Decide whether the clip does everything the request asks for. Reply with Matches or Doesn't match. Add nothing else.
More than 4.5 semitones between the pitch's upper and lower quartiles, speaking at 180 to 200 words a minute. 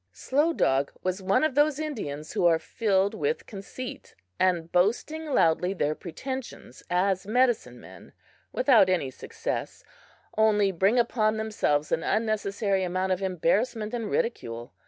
Doesn't match